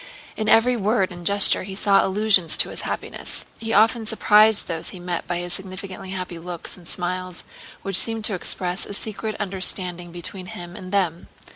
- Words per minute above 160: Yes, average, 180 wpm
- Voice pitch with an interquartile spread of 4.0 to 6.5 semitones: No, average, 2.9 semitones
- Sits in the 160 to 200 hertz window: Yes, high, 190 Hz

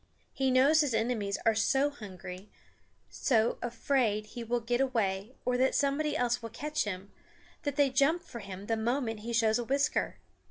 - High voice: Yes, high, 240 Hz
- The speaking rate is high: No, average, 175 wpm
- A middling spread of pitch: Yes, average, 3.8 semitones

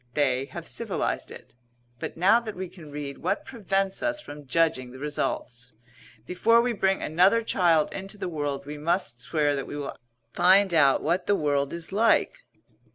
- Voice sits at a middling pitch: Yes, medium, 165 Hz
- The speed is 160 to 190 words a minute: Yes, average, 175 wpm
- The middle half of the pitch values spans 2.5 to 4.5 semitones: No, average, 5.3 semitones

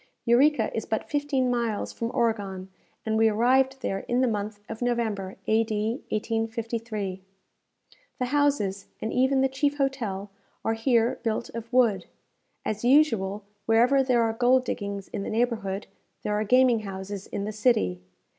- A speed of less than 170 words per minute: Yes, average, 155 wpm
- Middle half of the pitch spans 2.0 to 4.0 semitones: Yes, average, 3.5 semitones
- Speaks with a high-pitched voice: Yes, high, 225 Hz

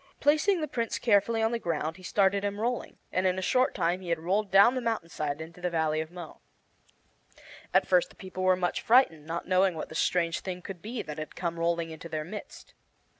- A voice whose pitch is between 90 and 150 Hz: No, medium, 185 Hz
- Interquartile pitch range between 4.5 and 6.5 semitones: Yes, average, 4.8 semitones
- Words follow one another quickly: Yes, fast, 225 wpm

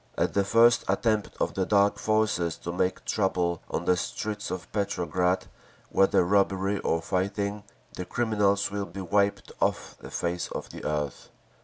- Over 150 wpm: Yes, average, 160 wpm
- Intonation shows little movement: Yes, narrow, 2.3 semitones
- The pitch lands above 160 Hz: No, low, 100 Hz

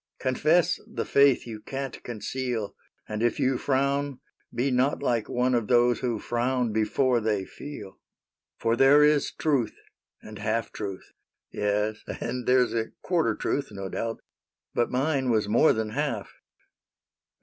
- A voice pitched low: Yes, low, 120 Hz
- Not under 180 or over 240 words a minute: No, average, 155 wpm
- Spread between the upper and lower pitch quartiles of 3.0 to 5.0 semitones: Yes, average, 3.6 semitones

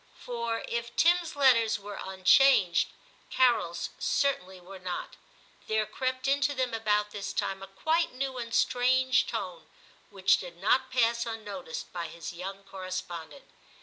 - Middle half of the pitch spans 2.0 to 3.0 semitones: No, wide, 5.4 semitones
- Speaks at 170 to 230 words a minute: No, average, 140 wpm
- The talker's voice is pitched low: No, high, 220 Hz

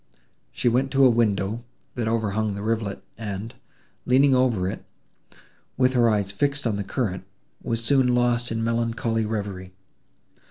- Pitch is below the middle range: Yes, low, 115 Hz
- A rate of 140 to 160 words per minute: Yes, average, 150 wpm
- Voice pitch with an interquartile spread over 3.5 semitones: No, average, 3.2 semitones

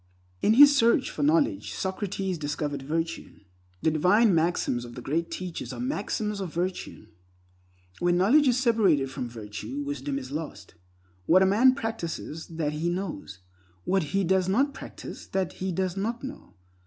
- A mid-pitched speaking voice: Yes, medium, 180 Hz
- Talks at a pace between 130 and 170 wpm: Yes, average, 160 wpm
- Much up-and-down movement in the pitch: Yes, wide, 6.1 semitones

